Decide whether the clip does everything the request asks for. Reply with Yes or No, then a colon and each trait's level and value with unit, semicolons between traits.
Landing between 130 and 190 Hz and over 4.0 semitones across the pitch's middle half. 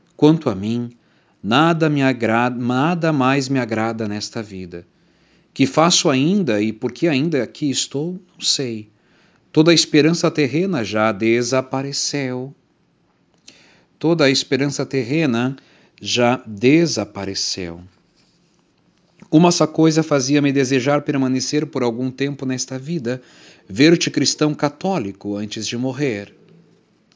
Yes: low, 135 Hz; average, 4.6 semitones